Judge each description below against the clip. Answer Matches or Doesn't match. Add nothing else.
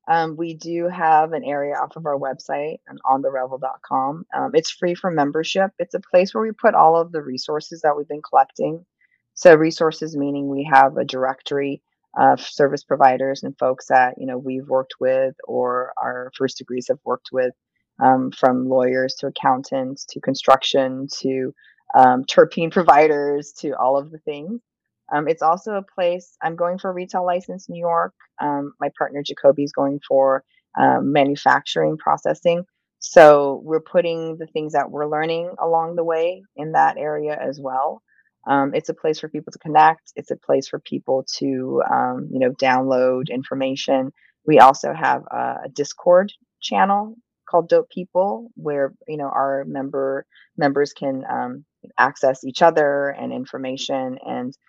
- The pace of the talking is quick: Doesn't match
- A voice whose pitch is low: Doesn't match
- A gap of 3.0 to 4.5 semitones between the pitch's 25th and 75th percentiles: Matches